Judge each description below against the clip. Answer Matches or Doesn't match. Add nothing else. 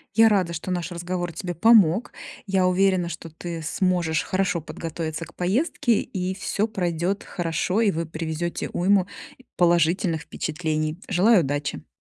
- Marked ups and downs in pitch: Doesn't match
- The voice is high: Doesn't match